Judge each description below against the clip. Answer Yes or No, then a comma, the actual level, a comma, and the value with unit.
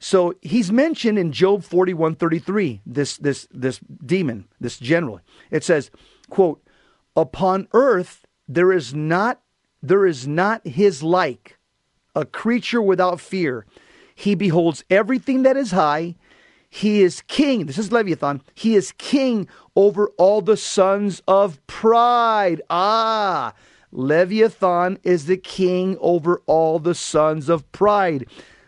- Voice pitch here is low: No, medium, 185 Hz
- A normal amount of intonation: Yes, average, 4.0 semitones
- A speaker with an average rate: No, slow, 130 wpm